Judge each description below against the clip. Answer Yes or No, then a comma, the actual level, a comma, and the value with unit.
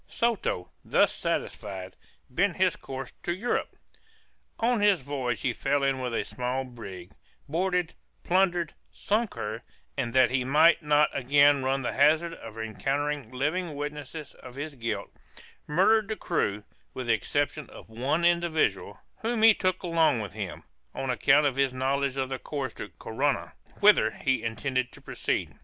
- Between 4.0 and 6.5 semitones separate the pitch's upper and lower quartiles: Yes, average, 5.1 semitones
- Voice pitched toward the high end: No, medium, 140 Hz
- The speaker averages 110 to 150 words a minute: No, average, 160 wpm